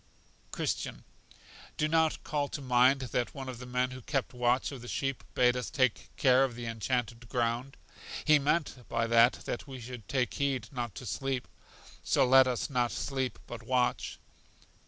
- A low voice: Yes, low, 125 Hz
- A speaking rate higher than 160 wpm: Yes, average, 180 wpm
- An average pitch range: No, narrow, 1.9 semitones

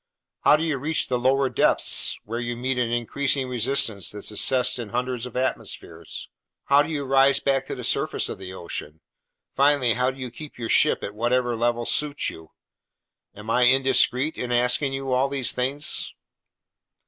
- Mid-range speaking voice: No, low, 125 Hz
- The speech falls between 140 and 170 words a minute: No, average, 180 wpm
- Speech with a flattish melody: Yes, narrow, 2.3 semitones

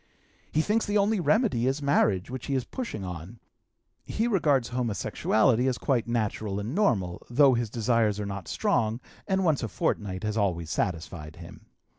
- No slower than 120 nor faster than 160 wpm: No, average, 170 wpm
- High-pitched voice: No, low, 115 Hz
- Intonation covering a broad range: Yes, wide, 5.8 semitones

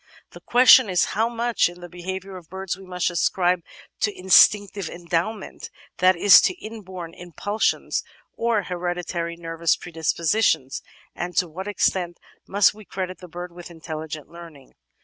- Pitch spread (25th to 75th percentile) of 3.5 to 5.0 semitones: No, narrow, 2.6 semitones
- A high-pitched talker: No, medium, 180 Hz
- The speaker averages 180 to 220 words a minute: No, average, 150 wpm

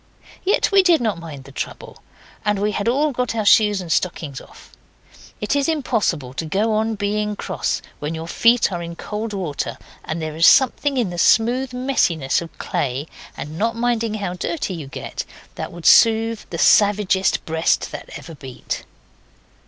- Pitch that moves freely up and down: Yes, wide, 5.7 semitones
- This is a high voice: Yes, high, 205 Hz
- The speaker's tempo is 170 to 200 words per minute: Yes, average, 175 wpm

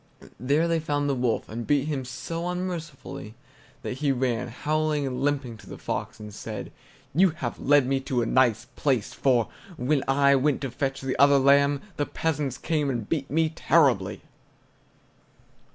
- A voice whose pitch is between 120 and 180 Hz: Yes, medium, 140 Hz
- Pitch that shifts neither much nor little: Yes, average, 3.0 semitones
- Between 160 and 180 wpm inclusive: Yes, average, 170 wpm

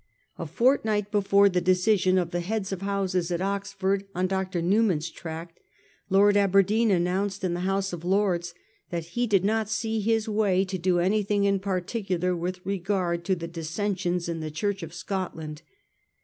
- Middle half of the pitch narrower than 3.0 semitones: Yes, narrow, 2.5 semitones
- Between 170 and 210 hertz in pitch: Yes, high, 190 Hz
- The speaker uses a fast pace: No, average, 170 wpm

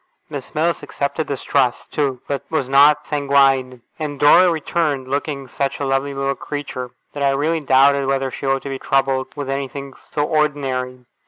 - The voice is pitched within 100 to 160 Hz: Yes, medium, 140 Hz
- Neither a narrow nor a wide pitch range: No, narrow, 1.4 semitones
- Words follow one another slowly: No, average, 175 wpm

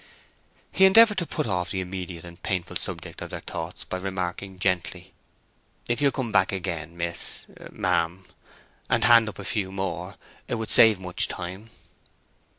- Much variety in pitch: No, average, 3.6 semitones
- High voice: No, very low, 95 Hz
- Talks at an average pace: Yes, average, 155 wpm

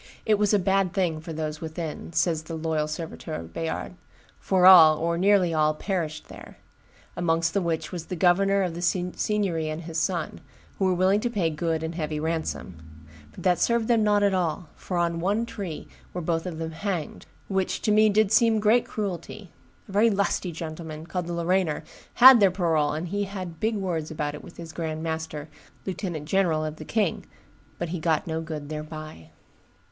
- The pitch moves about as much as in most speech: Yes, average, 3.5 semitones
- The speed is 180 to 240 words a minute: Yes, average, 195 wpm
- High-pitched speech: No, medium, 170 Hz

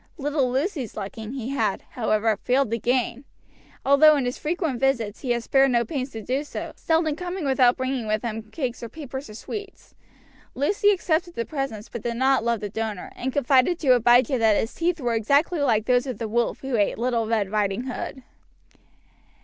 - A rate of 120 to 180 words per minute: No, average, 195 wpm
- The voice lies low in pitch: No, very high, 255 Hz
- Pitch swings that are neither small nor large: Yes, average, 3.7 semitones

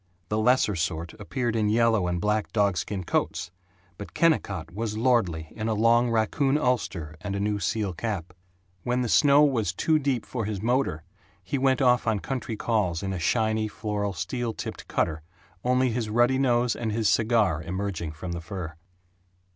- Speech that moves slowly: No, average, 175 wpm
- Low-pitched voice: Yes, low, 110 Hz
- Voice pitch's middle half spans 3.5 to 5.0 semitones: Yes, average, 4.5 semitones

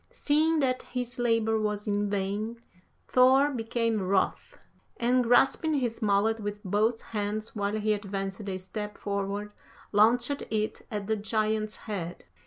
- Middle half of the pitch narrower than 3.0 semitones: Yes, narrow, 2.6 semitones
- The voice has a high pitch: Yes, high, 215 Hz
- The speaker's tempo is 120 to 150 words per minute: Yes, average, 140 wpm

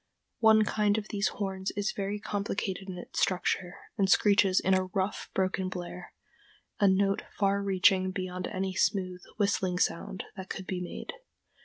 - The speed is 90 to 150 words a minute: No, average, 160 wpm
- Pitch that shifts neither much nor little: No, narrow, 1.4 semitones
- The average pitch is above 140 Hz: Yes, high, 190 Hz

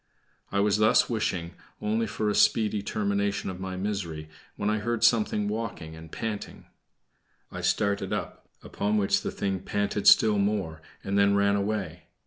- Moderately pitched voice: No, low, 100 Hz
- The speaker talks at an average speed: Yes, average, 160 wpm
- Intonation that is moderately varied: No, narrow, 1.7 semitones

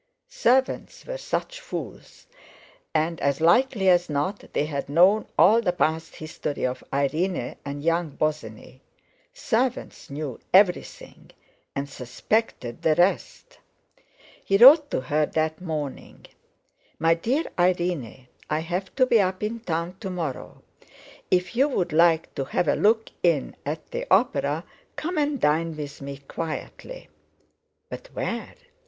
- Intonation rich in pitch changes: Yes, wide, 6.2 semitones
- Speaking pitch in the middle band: Yes, medium, 170 Hz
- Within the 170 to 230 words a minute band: No, slow, 135 wpm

